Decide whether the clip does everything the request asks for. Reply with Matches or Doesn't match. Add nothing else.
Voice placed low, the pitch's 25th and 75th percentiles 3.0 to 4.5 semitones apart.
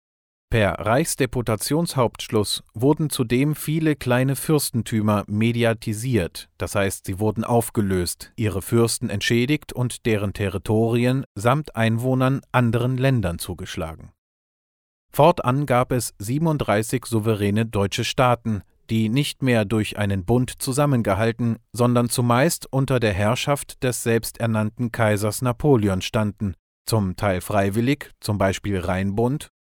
Matches